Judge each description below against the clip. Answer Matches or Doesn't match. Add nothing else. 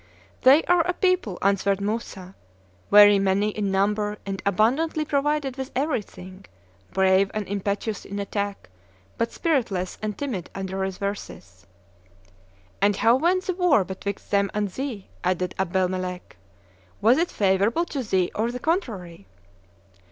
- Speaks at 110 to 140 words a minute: Matches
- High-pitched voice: Matches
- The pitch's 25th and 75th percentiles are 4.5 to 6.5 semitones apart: Matches